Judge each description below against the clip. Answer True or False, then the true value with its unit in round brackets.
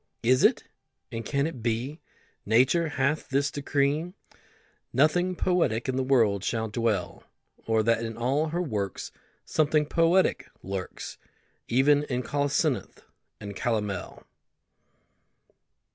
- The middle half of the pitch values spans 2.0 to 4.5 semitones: False (4.9 semitones)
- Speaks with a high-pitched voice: False (130 Hz)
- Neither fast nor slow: False (115 wpm)